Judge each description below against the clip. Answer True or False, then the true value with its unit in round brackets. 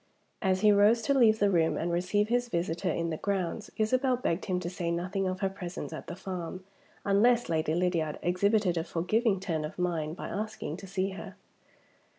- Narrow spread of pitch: False (3.6 semitones)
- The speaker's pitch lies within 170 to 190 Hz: True (185 Hz)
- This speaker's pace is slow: False (195 wpm)